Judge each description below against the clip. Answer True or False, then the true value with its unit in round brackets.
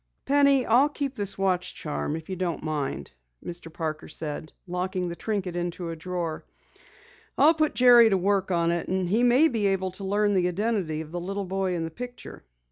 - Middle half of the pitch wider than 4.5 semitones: False (4.2 semitones)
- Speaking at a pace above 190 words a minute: True (200 wpm)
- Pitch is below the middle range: False (185 Hz)